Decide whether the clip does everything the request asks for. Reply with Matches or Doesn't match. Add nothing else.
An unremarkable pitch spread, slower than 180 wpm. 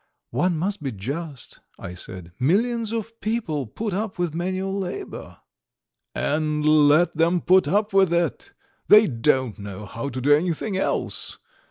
Doesn't match